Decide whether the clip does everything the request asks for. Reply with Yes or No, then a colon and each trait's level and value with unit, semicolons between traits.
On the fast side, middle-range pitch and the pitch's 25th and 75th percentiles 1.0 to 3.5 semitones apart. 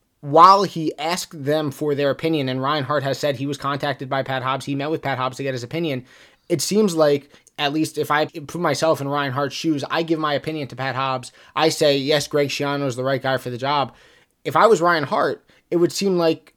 Yes: fast, 245 wpm; medium, 145 Hz; narrow, 2.5 semitones